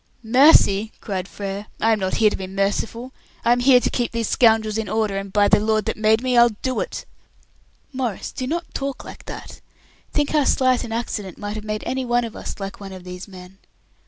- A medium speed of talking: No, fast, 220 wpm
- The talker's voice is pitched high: Yes, high, 220 Hz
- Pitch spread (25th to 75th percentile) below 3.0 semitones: No, average, 3.5 semitones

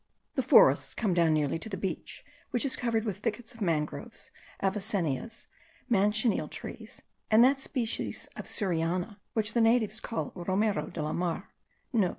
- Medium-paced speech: Yes, average, 155 wpm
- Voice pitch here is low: No, high, 210 Hz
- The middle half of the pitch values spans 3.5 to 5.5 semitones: Yes, average, 4.3 semitones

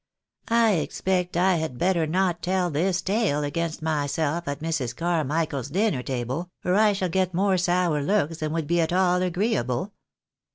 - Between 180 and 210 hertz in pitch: No, medium, 170 Hz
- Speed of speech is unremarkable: Yes, average, 165 wpm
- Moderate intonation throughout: Yes, average, 3.4 semitones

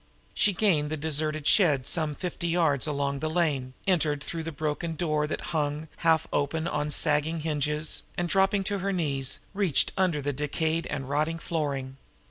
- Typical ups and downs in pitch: No, narrow, 2.3 semitones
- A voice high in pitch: No, medium, 155 Hz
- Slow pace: No, average, 175 wpm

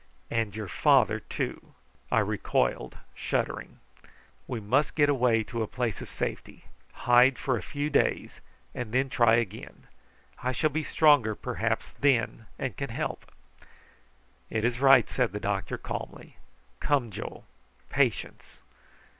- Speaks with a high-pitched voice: No, low, 125 Hz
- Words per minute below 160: Yes, average, 140 wpm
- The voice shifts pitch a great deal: No, average, 3.5 semitones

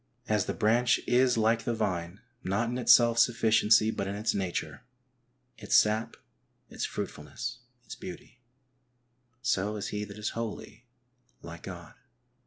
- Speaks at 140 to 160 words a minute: Yes, average, 145 wpm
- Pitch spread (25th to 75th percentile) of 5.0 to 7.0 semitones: No, narrow, 2.5 semitones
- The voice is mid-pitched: No, low, 110 Hz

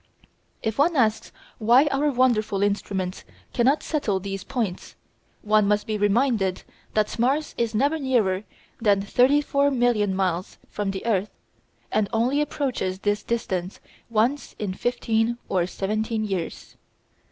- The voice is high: Yes, high, 215 Hz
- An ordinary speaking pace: No, slow, 130 wpm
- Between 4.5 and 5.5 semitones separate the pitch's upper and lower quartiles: No, average, 4.1 semitones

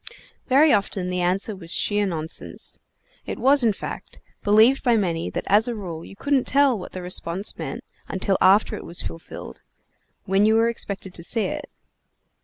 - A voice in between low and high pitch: No, high, 200 Hz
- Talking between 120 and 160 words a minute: No, average, 180 wpm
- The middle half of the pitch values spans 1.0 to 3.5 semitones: No, average, 4.1 semitones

